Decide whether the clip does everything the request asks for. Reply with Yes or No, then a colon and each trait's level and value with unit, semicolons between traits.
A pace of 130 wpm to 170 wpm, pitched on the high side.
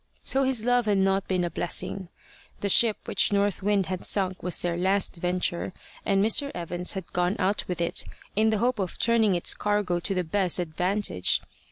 No: average, 195 wpm; high, 195 Hz